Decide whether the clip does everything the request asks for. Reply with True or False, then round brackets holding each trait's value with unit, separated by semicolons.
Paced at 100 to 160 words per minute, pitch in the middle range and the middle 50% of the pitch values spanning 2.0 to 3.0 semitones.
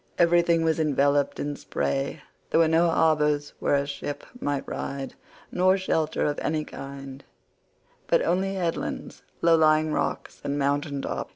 True (150 wpm; 150 Hz; 2.7 semitones)